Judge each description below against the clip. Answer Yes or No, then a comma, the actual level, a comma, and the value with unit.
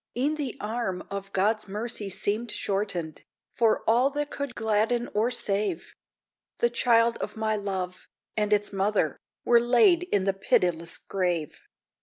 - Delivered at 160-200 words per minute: No, average, 145 wpm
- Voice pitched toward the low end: No, high, 215 Hz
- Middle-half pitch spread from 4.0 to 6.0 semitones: No, average, 3.5 semitones